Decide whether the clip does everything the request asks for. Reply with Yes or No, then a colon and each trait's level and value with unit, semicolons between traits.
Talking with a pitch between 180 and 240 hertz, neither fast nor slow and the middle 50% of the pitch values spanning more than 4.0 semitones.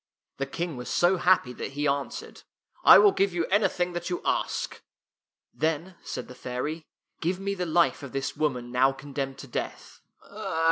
No: medium, 155 Hz; average, 190 wpm; average, 4.6 semitones